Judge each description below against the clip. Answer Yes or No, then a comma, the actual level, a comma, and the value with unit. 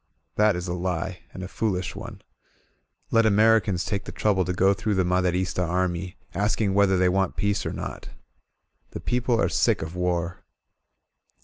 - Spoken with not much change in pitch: Yes, narrow, 2.3 semitones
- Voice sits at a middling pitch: No, very low, 95 Hz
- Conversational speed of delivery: Yes, average, 170 wpm